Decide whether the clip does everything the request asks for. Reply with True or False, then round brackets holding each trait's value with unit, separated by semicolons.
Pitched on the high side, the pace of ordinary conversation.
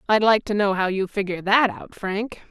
False (200 Hz; 240 wpm)